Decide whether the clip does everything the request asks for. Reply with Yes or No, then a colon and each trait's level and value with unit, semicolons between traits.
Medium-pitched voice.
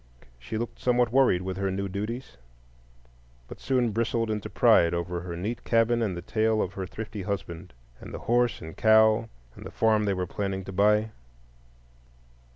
No: low, 105 Hz